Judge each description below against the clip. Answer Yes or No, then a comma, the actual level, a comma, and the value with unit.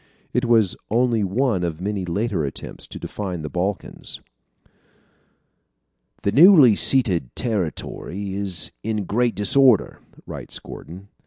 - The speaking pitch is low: Yes, low, 100 Hz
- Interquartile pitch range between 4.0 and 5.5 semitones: Yes, average, 4.7 semitones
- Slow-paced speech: Yes, slow, 115 wpm